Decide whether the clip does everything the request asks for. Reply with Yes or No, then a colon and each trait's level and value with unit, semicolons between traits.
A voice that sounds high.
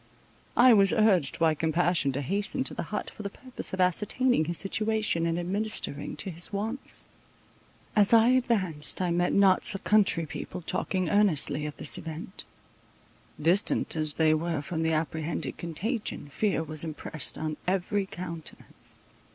No: medium, 175 Hz